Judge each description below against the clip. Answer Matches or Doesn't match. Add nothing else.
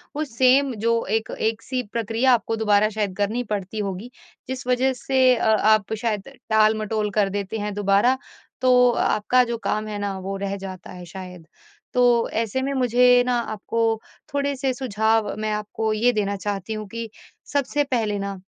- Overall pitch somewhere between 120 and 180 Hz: Doesn't match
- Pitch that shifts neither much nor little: Matches